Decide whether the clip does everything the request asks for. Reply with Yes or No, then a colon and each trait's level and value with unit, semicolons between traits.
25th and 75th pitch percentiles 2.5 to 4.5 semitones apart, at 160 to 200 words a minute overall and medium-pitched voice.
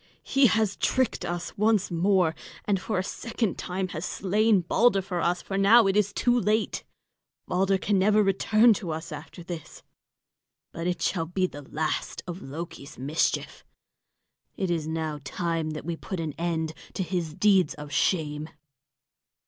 Yes: average, 3.8 semitones; average, 165 wpm; medium, 180 Hz